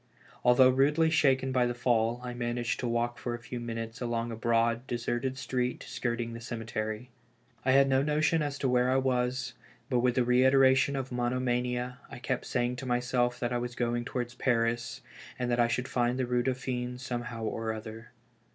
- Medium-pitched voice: No, low, 125 Hz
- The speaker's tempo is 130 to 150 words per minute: No, average, 195 wpm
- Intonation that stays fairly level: Yes, narrow, 1.4 semitones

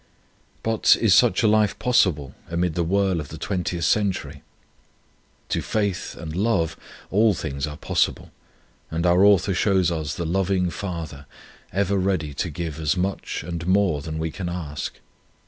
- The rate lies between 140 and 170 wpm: Yes, average, 160 wpm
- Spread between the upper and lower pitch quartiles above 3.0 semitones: Yes, average, 3.7 semitones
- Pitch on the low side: Yes, very low, 90 Hz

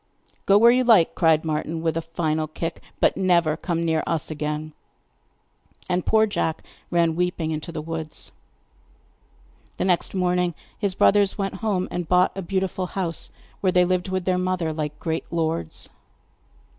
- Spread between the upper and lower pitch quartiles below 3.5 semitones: Yes, narrow, 2.6 semitones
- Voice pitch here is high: No, medium, 175 Hz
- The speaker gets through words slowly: No, average, 160 wpm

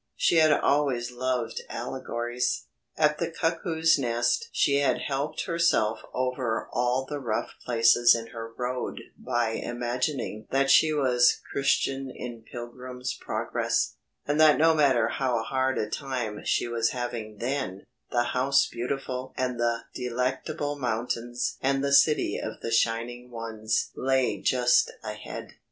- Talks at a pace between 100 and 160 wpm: Yes, average, 140 wpm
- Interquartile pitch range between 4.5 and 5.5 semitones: No, narrow, 2.6 semitones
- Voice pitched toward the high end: No, low, 125 Hz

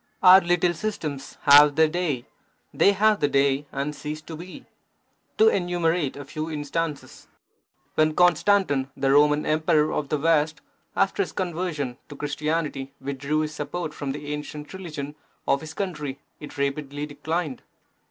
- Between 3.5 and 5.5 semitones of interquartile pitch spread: No, average, 3.0 semitones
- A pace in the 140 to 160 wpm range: Yes, average, 150 wpm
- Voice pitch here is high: No, medium, 150 Hz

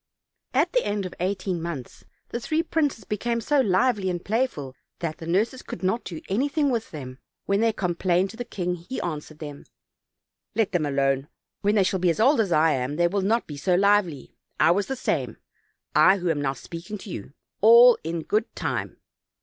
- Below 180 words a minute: No, fast, 205 wpm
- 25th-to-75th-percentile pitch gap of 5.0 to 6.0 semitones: Yes, wide, 5.4 semitones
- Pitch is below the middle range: No, high, 190 Hz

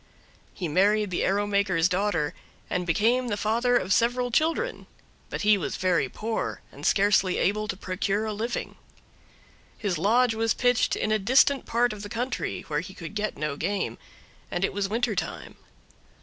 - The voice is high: Yes, high, 205 Hz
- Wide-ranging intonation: No, average, 3.7 semitones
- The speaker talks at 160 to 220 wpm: Yes, average, 175 wpm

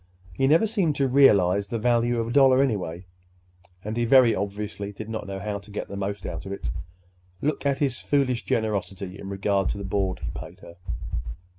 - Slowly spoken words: No, average, 200 wpm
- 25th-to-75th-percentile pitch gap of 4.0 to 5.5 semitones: Yes, average, 4.6 semitones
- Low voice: Yes, low, 105 Hz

